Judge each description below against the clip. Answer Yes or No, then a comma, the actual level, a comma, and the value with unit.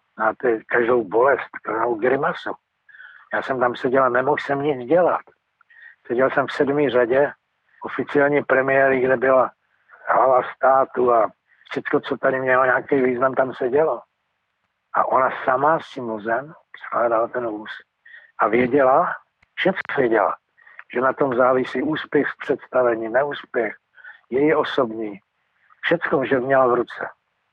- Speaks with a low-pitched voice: Yes, low, 130 Hz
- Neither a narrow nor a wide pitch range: No, narrow, 2.0 semitones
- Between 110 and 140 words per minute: Yes, average, 135 wpm